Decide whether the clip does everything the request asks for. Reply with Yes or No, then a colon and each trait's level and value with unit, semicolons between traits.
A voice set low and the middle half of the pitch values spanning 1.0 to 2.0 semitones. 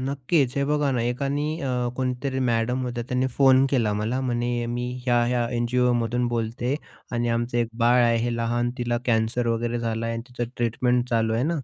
Yes: low, 120 Hz; narrow, 1.5 semitones